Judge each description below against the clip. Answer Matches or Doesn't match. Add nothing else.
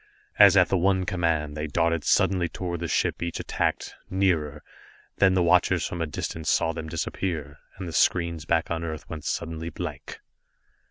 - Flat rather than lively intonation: Matches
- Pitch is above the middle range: Doesn't match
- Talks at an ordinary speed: Matches